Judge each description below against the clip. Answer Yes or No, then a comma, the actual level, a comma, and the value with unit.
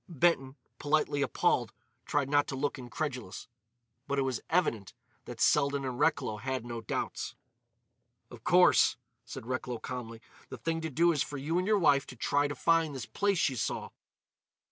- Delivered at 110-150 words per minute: No, average, 170 wpm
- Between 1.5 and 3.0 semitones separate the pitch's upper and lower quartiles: No, average, 3.7 semitones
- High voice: No, medium, 140 Hz